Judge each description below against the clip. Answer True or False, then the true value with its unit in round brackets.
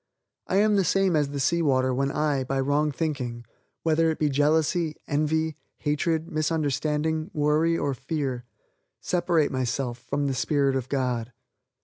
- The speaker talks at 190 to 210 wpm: False (150 wpm)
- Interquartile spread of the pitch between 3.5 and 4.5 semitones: False (3.0 semitones)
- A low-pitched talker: False (150 Hz)